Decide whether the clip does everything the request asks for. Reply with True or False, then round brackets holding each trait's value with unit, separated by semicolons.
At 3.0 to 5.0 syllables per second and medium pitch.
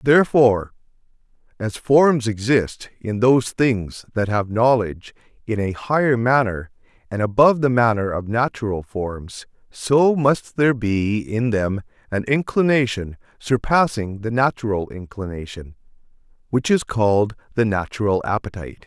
False (4.6 syllables/s; 115 Hz)